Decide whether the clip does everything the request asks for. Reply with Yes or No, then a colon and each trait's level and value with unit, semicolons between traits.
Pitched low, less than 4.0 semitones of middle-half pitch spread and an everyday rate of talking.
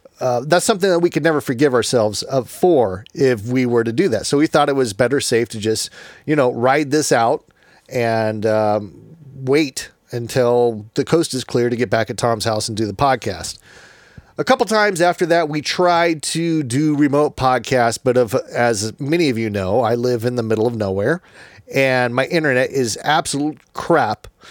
No: low, 130 Hz; average, 4.5 semitones; average, 195 wpm